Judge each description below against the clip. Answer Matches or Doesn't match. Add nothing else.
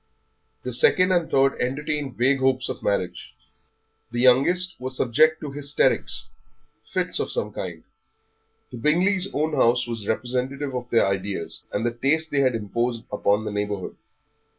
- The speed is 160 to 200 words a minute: Doesn't match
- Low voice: Matches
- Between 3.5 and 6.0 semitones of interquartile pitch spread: Matches